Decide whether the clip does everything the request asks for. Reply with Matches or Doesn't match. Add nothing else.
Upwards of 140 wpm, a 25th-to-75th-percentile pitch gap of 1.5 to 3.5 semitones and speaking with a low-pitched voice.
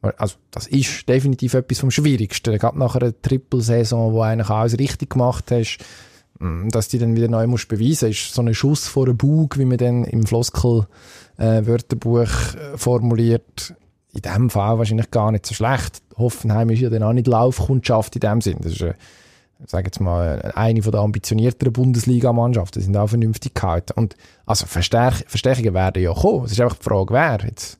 Matches